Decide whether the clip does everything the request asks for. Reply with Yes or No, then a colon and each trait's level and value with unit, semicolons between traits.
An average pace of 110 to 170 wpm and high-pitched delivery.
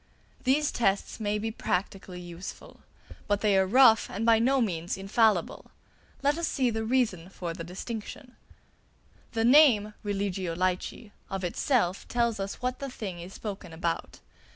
Yes: average, 150 wpm; high, 205 Hz